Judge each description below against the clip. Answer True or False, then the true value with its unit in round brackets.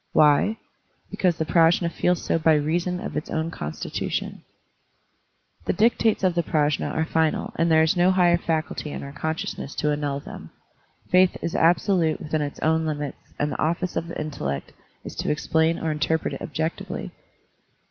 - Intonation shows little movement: True (2.3 semitones)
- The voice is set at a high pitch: False (160 Hz)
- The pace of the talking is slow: False (170 wpm)